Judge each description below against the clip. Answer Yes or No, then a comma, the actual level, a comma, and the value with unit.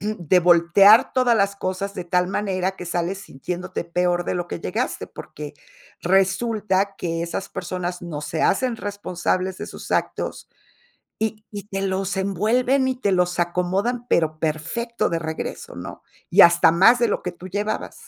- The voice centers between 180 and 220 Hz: Yes, medium, 185 Hz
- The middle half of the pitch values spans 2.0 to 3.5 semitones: Yes, average, 2.9 semitones